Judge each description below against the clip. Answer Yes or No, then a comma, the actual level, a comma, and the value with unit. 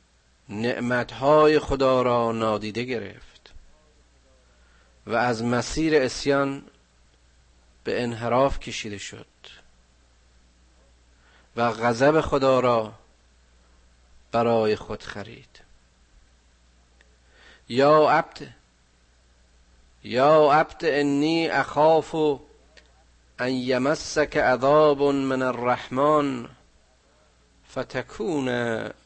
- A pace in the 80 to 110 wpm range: No, slow, 70 wpm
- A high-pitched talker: No, low, 110 Hz